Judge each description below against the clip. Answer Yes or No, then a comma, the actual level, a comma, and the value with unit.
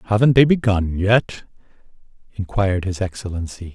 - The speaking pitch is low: Yes, low, 100 Hz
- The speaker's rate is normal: No, slow, 110 wpm